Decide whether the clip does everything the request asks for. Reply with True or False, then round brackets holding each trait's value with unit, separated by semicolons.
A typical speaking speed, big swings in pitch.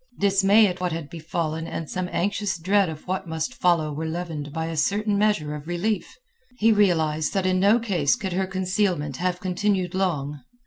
False (185 wpm; 3.6 semitones)